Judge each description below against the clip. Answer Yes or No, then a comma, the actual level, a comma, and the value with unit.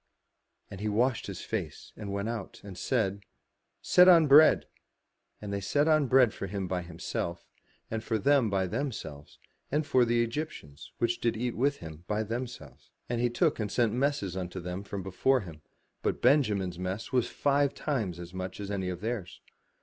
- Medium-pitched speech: No, low, 105 Hz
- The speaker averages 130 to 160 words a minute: No, average, 185 wpm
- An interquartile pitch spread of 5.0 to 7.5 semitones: Yes, average, 5.3 semitones